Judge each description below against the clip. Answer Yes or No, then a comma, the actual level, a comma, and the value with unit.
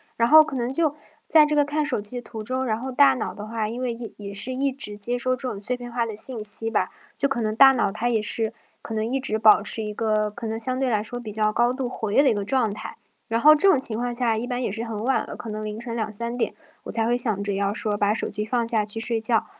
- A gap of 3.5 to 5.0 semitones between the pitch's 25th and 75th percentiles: No, average, 2.9 semitones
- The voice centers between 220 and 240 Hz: Yes, high, 230 Hz